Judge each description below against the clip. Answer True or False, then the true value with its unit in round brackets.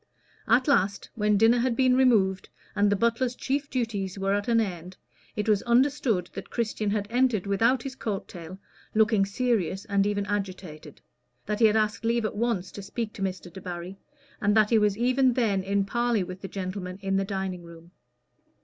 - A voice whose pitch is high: True (205 Hz)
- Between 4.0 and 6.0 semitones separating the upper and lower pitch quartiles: False (3.5 semitones)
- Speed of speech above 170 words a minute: True (190 wpm)